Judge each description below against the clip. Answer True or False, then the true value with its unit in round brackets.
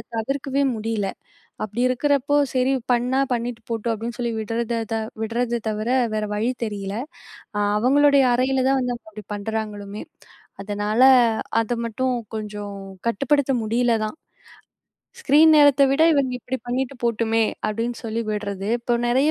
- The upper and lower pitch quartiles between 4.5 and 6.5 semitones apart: False (3.2 semitones)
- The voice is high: True (235 Hz)